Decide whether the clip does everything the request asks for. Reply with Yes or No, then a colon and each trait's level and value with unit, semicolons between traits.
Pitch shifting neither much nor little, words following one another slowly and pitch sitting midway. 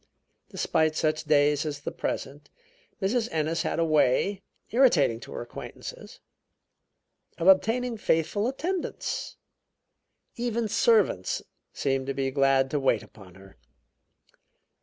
No: wide, 7.8 semitones; slow, 115 wpm; medium, 155 Hz